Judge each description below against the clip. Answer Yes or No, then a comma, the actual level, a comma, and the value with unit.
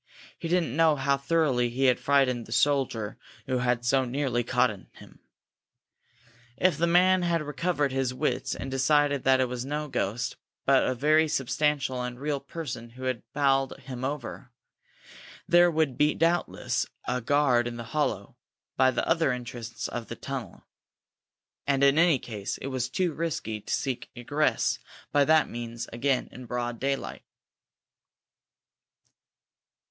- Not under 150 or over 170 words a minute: Yes, average, 155 wpm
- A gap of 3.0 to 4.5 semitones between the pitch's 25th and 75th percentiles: Yes, average, 3.4 semitones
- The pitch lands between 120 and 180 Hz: Yes, low, 135 Hz